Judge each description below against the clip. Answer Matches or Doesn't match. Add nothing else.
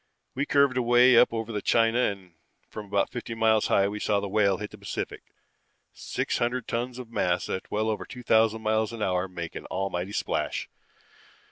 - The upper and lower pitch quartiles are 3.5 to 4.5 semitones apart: Doesn't match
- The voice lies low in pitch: Matches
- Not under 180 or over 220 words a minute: Matches